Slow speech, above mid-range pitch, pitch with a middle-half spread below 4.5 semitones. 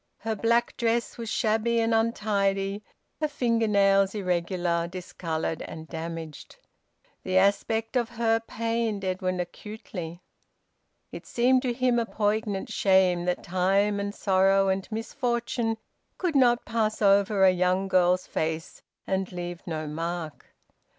Yes: slow, 130 wpm; high, 200 Hz; average, 3.9 semitones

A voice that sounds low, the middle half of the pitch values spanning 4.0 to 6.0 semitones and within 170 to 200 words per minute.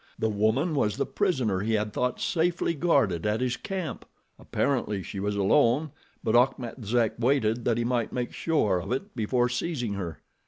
Yes: low, 120 Hz; average, 4.8 semitones; average, 180 wpm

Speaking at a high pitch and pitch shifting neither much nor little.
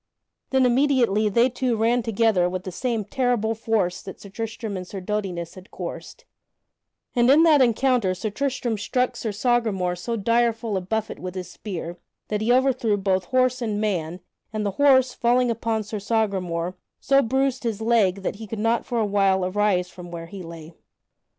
Yes: high, 220 Hz; average, 4.2 semitones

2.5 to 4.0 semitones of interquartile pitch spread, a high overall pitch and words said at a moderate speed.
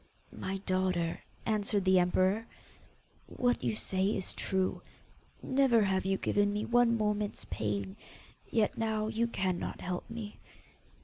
No: average, 3.0 semitones; high, 205 Hz; slow, 130 wpm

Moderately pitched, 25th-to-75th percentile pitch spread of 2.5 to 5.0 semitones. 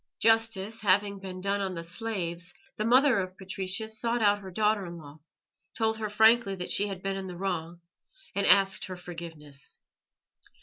No: high, 195 Hz; average, 3.3 semitones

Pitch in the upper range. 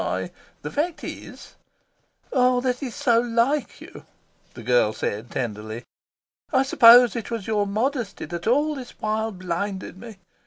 Yes: high, 230 Hz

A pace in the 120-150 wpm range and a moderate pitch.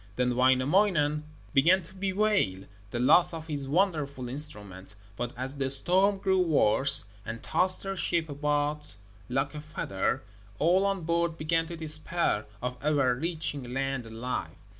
Yes: average, 145 wpm; medium, 150 Hz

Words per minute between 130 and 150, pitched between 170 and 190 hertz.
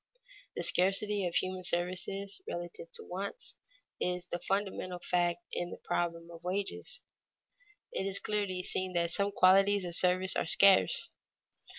Yes: average, 145 wpm; medium, 185 Hz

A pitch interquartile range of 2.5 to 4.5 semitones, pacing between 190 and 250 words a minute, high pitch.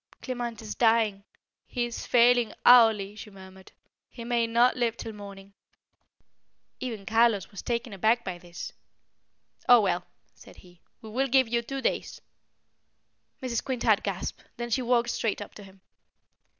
No: average, 3.2 semitones; average, 150 wpm; high, 225 Hz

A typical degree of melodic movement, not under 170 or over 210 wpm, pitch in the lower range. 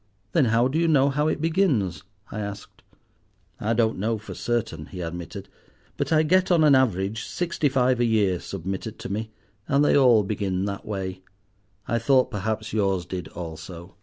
No: wide, 5.9 semitones; average, 180 wpm; low, 110 Hz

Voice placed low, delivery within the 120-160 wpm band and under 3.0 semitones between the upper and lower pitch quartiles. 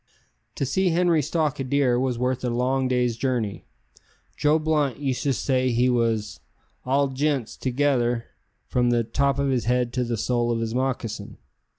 No: low, 130 Hz; average, 175 wpm; narrow, 2.6 semitones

